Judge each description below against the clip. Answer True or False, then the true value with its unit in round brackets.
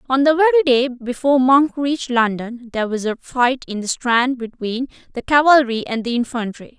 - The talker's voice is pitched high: True (255 Hz)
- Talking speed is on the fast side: False (185 wpm)